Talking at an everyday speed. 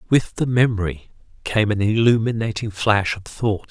Yes: average, 160 wpm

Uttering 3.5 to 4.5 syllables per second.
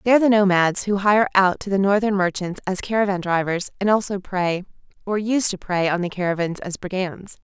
No: 5.4 syllables/s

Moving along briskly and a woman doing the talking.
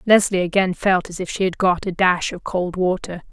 Yes: fast, 235 wpm; female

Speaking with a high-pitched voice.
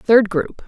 Yes: high, 200 Hz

